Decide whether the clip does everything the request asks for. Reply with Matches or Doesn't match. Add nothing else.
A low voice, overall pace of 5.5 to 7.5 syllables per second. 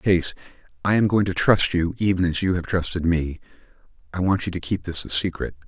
Matches